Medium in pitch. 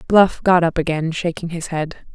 Yes: medium, 170 Hz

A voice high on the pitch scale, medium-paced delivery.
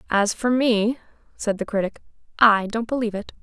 Yes: high, 220 Hz; average, 175 wpm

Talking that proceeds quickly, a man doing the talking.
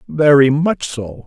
No: average, 140 wpm; male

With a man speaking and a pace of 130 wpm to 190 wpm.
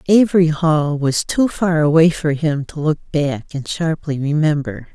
No: female; average, 170 wpm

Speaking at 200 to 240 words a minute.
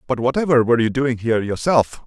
Yes: fast, 205 wpm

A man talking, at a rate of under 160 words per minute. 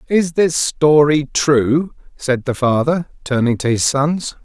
Yes: male; average, 150 wpm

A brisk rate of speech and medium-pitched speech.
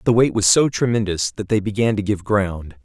No: fast, 255 wpm; low, 100 Hz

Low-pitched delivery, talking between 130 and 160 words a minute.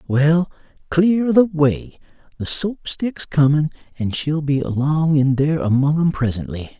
No: medium, 150 Hz; average, 150 wpm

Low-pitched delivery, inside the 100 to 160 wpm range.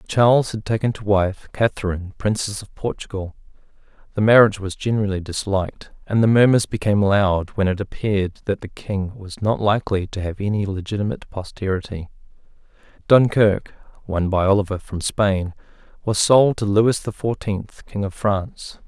Yes: low, 100 Hz; average, 155 wpm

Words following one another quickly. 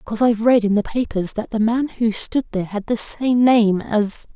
Yes: fast, 235 wpm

